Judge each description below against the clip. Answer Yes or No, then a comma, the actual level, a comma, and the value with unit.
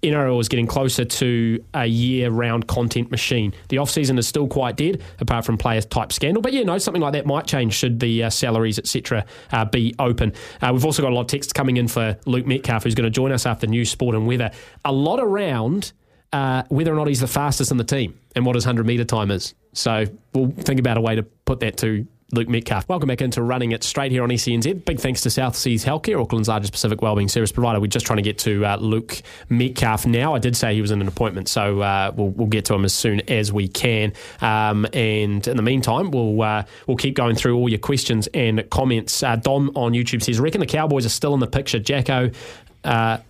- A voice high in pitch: No, low, 120 Hz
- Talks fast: Yes, fast, 240 wpm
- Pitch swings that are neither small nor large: Yes, average, 3.0 semitones